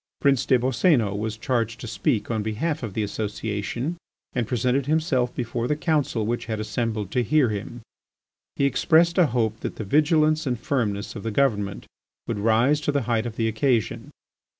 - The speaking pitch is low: Yes, low, 120 Hz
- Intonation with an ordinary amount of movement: Yes, average, 4.2 semitones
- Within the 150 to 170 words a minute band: No, average, 180 wpm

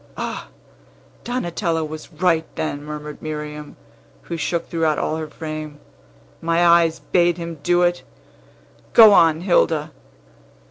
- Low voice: No, medium, 160 Hz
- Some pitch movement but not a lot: No, narrow, 2.1 semitones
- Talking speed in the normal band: No, slow, 125 wpm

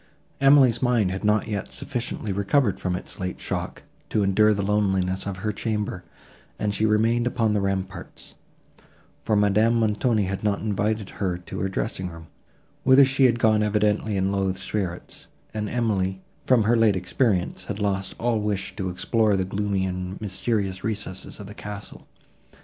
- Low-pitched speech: Yes, low, 105 Hz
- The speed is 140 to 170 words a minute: Yes, average, 165 wpm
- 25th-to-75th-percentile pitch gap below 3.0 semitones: Yes, narrow, 2.4 semitones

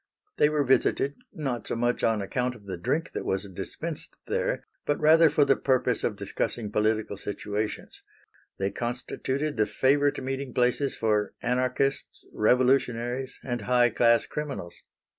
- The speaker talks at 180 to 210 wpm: No, average, 145 wpm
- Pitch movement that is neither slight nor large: Yes, average, 4.1 semitones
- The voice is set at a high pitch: No, low, 125 Hz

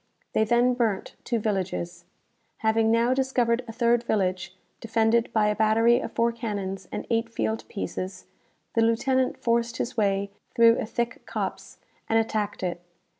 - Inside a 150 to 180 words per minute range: Yes, average, 155 wpm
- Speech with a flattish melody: Yes, narrow, 2.3 semitones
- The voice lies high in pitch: Yes, high, 225 Hz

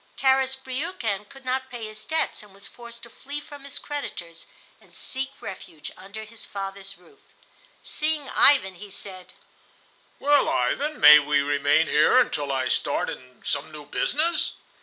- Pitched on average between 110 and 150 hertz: No, high, 220 Hz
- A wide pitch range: Yes, wide, 7.6 semitones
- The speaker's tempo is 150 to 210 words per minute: Yes, average, 160 wpm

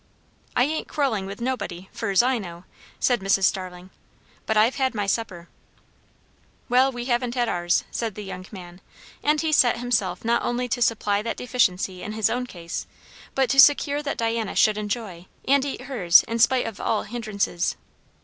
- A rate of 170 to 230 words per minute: Yes, average, 180 wpm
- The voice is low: No, high, 225 Hz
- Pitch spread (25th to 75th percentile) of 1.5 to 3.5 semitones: No, average, 4.3 semitones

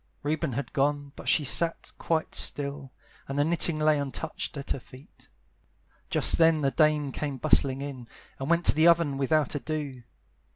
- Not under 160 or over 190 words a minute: Yes, average, 170 wpm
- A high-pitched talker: No, medium, 145 Hz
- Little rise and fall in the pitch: Yes, narrow, 2.3 semitones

